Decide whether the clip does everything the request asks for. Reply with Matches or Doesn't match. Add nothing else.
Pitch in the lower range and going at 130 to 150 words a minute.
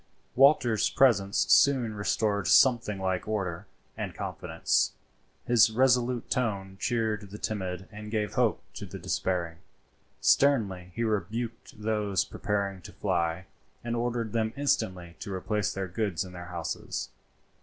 Matches